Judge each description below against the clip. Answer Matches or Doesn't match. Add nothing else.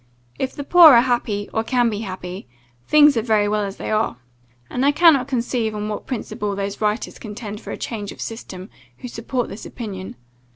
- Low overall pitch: Doesn't match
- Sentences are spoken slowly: Doesn't match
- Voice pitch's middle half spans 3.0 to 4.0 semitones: Matches